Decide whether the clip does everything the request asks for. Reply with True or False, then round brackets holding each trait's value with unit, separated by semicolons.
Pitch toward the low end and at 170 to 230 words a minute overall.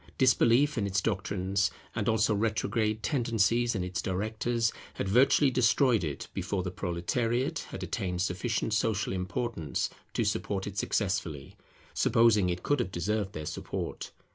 False (105 Hz; 140 wpm)